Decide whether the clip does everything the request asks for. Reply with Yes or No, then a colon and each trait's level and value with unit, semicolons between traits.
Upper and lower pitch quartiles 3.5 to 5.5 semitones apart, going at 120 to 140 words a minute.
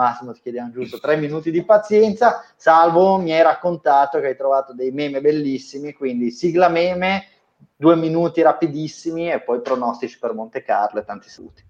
No: average, 4.9 semitones; fast, 170 wpm